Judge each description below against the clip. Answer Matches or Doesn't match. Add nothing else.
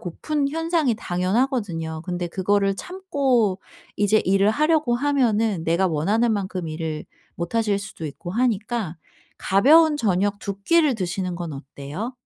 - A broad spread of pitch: Matches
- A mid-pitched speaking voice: Doesn't match